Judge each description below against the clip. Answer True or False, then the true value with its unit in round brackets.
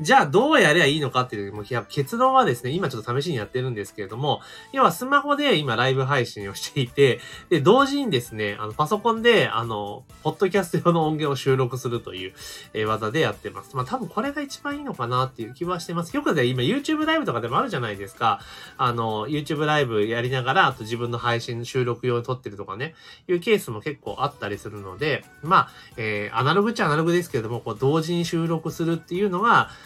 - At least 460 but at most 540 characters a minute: True (490 characters per minute)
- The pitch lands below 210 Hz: True (135 Hz)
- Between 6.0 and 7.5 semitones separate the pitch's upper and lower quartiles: True (7.0 semitones)